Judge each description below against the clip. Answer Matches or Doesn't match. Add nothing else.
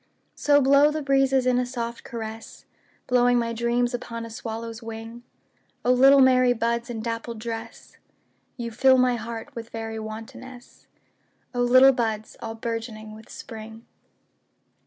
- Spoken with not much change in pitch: Matches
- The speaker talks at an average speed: Doesn't match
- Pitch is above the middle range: Matches